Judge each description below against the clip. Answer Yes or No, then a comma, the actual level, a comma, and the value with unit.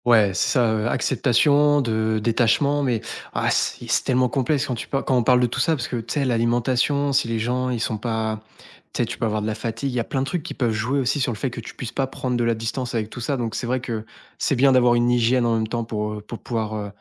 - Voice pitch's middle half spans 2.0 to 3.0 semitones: Yes, narrow, 2.6 semitones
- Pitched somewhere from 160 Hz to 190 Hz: No, low, 120 Hz